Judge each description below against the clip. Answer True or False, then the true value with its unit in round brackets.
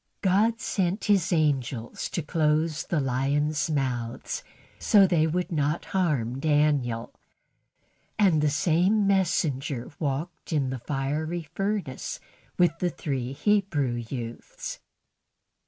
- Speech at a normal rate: False (110 wpm)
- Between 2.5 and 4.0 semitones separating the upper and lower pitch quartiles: False (4.7 semitones)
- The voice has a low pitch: False (155 Hz)